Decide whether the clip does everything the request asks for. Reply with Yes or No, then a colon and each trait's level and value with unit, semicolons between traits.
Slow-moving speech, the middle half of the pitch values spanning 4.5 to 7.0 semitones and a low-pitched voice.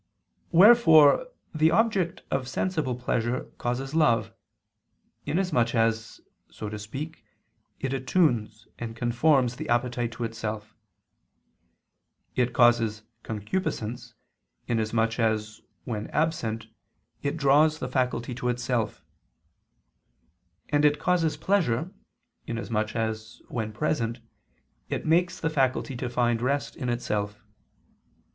Yes: slow, 110 wpm; average, 4.8 semitones; low, 120 Hz